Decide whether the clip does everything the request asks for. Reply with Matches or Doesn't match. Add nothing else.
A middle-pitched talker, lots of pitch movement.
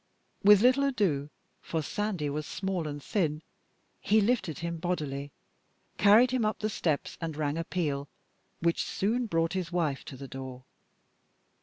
Matches